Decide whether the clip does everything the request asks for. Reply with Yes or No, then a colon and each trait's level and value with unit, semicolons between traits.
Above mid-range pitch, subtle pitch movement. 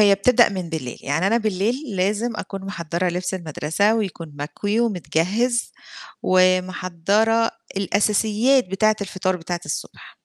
No: high, 195 Hz; average, 3.4 semitones